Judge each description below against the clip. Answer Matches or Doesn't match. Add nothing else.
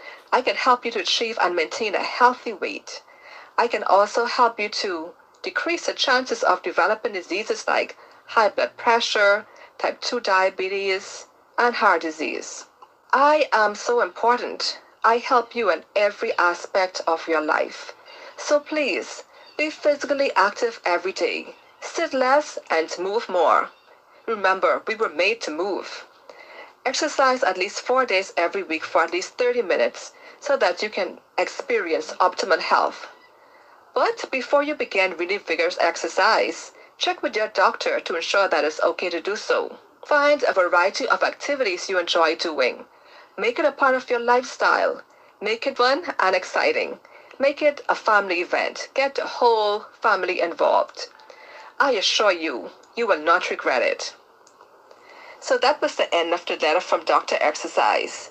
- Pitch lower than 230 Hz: Doesn't match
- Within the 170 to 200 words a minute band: Doesn't match